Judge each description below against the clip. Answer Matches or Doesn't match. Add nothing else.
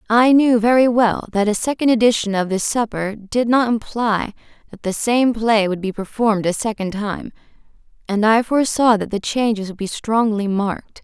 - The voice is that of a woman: Matches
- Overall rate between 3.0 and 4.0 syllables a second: Doesn't match